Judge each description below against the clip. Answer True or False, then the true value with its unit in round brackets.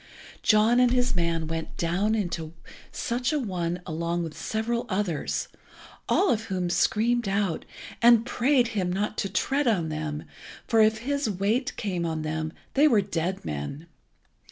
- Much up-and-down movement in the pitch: True (5.8 semitones)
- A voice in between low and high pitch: False (200 Hz)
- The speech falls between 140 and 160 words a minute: True (155 wpm)